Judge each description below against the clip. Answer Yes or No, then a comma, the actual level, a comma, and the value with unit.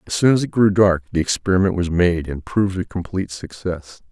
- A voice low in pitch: Yes, very low, 90 Hz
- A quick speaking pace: Yes, fast, 220 wpm